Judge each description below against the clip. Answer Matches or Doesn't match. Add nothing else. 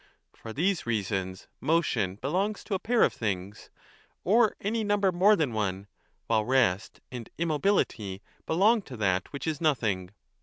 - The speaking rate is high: Doesn't match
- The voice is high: Doesn't match